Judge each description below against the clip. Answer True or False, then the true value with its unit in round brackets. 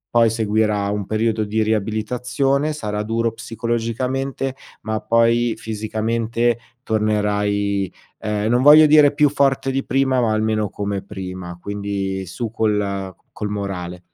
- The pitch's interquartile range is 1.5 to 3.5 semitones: True (2.6 semitones)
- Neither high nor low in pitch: False (110 Hz)